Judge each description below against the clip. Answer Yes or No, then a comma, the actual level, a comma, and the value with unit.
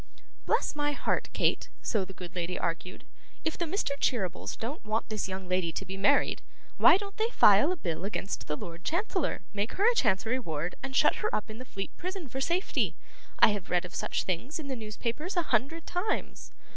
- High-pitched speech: Yes, high, 225 Hz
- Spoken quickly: Yes, fast, 210 wpm